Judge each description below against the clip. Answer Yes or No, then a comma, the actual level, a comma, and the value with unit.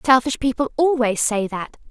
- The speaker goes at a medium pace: Yes, average, 155 wpm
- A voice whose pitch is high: Yes, very high, 250 Hz